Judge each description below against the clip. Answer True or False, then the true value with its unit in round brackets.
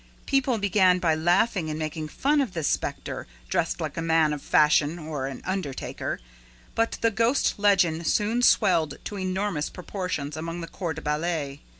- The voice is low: False (170 Hz)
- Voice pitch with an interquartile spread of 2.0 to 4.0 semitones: False (4.6 semitones)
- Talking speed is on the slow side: False (170 wpm)